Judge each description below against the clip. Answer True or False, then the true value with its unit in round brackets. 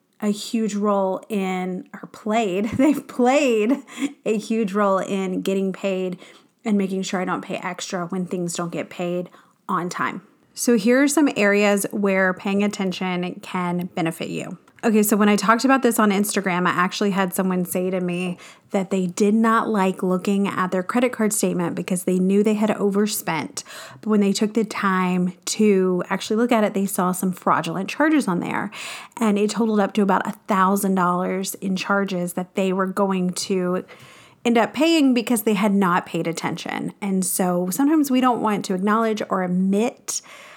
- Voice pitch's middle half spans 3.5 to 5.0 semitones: False (2.9 semitones)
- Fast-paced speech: False (185 wpm)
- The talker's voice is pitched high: True (200 Hz)